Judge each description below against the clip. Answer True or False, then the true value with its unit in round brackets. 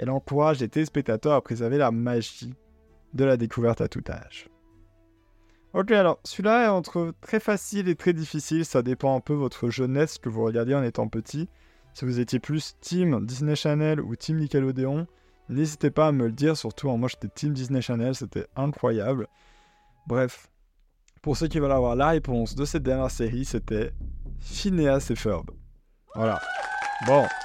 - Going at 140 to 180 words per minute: True (175 wpm)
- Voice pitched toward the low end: True (130 Hz)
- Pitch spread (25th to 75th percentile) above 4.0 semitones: True (5.0 semitones)